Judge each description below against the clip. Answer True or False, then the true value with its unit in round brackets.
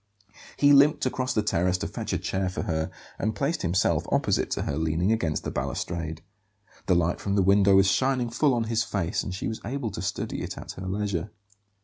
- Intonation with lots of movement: False (5.0 semitones)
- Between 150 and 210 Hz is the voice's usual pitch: False (100 Hz)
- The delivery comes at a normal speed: False (215 wpm)